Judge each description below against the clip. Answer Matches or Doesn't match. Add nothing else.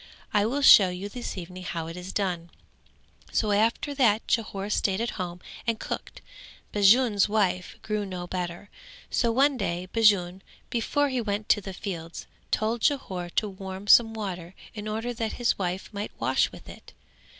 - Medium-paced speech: Matches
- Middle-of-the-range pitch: Doesn't match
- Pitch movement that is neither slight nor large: Matches